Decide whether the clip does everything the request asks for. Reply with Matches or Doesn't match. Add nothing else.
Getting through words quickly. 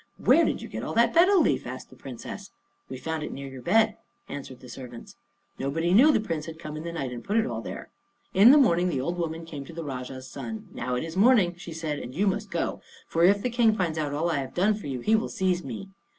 Matches